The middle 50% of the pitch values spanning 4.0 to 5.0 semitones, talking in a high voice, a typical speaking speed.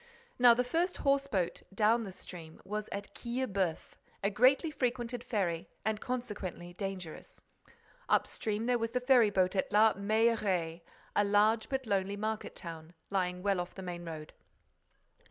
Yes: average, 4.4 semitones; high, 205 Hz; average, 155 wpm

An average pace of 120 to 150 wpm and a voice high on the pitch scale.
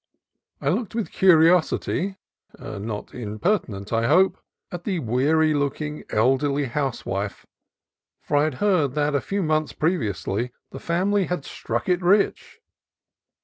No: average, 140 wpm; medium, 150 Hz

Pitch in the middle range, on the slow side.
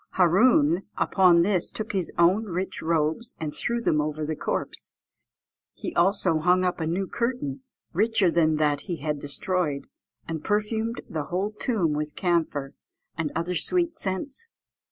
No: medium, 175 Hz; average, 155 wpm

